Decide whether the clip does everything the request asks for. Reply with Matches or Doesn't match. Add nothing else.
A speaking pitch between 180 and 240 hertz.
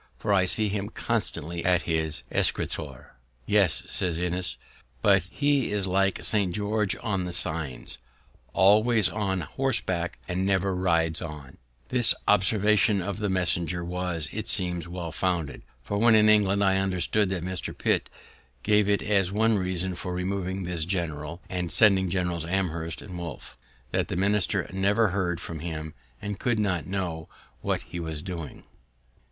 Doesn't match